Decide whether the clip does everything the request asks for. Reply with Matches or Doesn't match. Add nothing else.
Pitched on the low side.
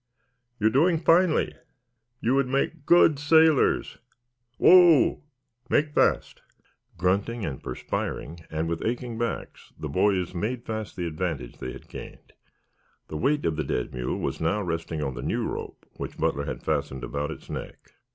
Matches